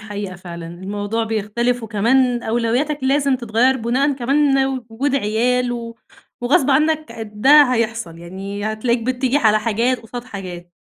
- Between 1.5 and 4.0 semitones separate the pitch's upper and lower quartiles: Yes, average, 3.7 semitones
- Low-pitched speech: No, high, 235 Hz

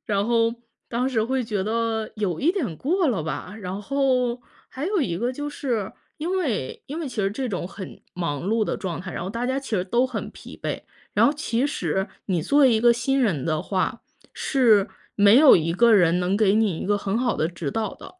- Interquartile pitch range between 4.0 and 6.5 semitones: Yes, wide, 5.4 semitones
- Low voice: No, high, 225 Hz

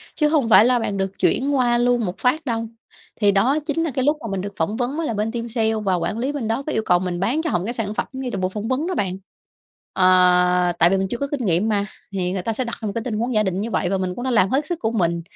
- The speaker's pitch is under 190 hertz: No, high, 225 Hz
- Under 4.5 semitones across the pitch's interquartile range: No, average, 4.9 semitones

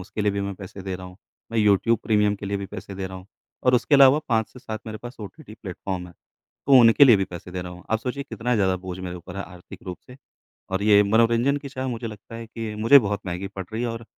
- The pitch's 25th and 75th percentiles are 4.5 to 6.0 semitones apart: No, average, 3.5 semitones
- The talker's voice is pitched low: Yes, low, 105 Hz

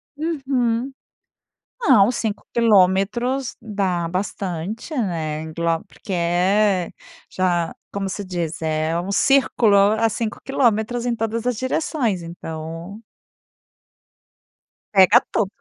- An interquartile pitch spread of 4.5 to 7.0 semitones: Yes, average, 5.0 semitones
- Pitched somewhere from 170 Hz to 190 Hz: No, high, 200 Hz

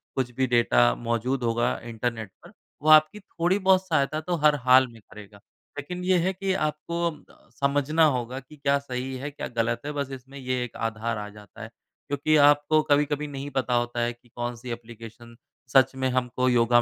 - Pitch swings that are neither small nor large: Yes, average, 3.8 semitones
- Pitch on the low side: Yes, low, 130 Hz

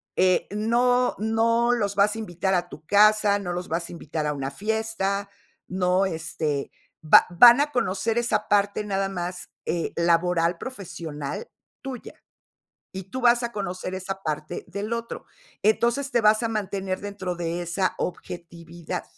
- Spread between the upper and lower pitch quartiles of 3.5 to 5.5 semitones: Yes, average, 4.1 semitones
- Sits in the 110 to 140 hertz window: No, high, 195 Hz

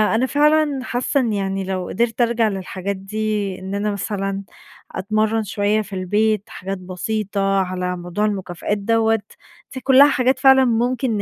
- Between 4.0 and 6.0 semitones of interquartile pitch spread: No, average, 3.4 semitones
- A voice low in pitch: No, high, 210 Hz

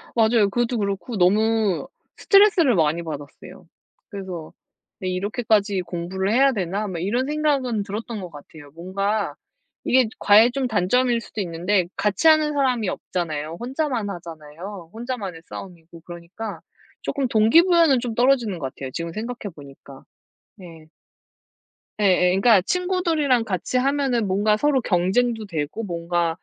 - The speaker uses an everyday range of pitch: No, wide, 5.9 semitones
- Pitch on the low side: No, high, 205 Hz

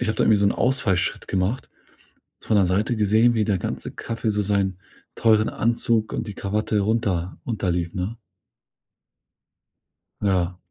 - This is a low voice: Yes, low, 105 Hz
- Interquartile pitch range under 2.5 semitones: No, average, 2.8 semitones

